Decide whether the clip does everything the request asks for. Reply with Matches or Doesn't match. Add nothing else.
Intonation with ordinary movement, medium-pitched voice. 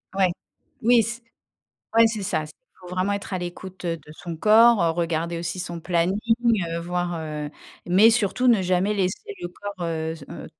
Matches